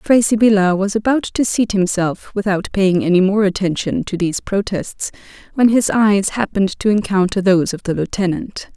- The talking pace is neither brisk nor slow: Yes, average, 170 wpm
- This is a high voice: Yes, high, 200 Hz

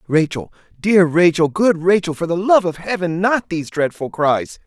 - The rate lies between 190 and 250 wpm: No, average, 180 wpm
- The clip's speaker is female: No, male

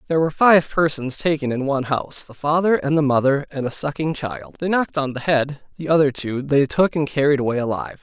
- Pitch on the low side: No, medium, 145 Hz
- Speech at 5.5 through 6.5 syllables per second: Yes, 6.0 syllables/s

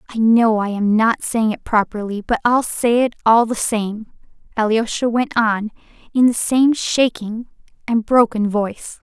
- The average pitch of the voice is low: No, high, 225 Hz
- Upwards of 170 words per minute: No, average, 165 wpm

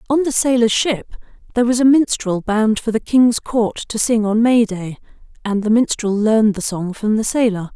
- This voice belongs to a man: No, female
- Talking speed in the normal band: No, fast, 210 wpm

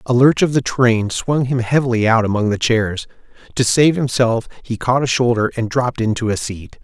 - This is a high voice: No, low, 120 Hz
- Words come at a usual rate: No, fast, 210 wpm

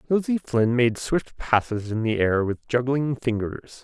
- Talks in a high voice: No, low, 125 Hz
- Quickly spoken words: No, average, 170 wpm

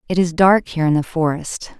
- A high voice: No, medium, 170 Hz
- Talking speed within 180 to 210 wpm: No, fast, 235 wpm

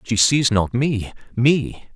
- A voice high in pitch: No, low, 120 Hz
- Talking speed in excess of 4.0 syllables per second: No, 3.2 syllables/s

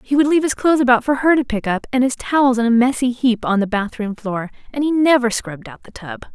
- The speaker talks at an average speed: No, fast, 275 wpm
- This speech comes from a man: No, female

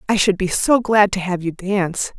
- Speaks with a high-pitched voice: Yes, high, 195 Hz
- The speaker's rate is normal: No, fast, 245 wpm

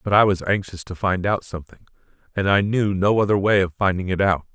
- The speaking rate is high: Yes, fast, 240 wpm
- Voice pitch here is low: Yes, very low, 95 Hz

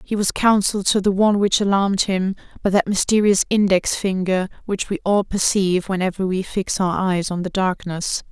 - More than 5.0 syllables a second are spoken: Yes, 5.3 syllables/s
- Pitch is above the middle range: Yes, high, 195 Hz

